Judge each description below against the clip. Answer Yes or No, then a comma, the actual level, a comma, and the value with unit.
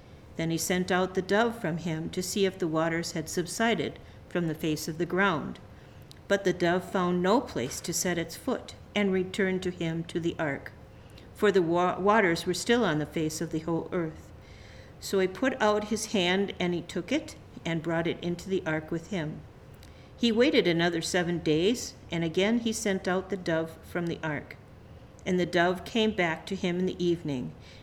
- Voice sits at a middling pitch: Yes, medium, 175 Hz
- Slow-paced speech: No, average, 200 wpm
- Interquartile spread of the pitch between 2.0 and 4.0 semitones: Yes, average, 2.9 semitones